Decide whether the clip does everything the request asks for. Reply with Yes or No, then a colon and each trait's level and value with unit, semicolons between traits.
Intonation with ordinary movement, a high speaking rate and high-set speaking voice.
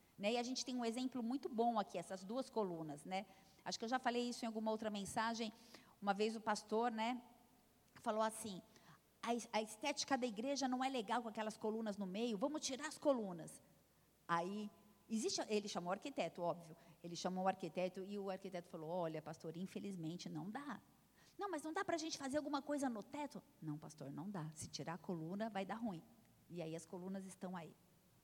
Yes: average, 4.7 semitones; fast, 200 wpm; high, 215 Hz